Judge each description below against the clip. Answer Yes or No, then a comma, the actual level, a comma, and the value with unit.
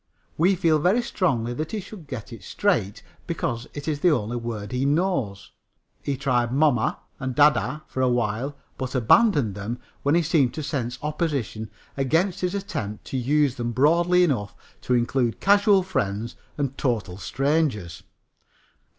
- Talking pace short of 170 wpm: Yes, average, 160 wpm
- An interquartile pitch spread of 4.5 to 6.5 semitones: Yes, wide, 5.5 semitones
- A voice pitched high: No, low, 135 Hz